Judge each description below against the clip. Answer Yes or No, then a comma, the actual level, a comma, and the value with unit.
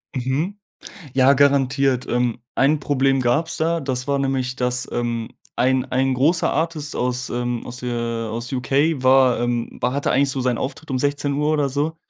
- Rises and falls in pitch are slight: Yes, narrow, 2.3 semitones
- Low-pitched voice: Yes, low, 130 Hz